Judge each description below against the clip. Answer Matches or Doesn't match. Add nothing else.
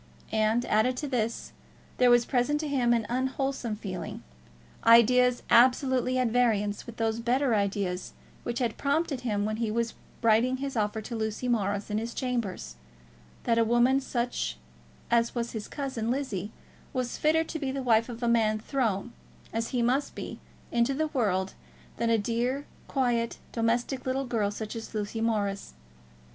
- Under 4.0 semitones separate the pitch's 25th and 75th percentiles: Matches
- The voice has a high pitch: Matches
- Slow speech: Doesn't match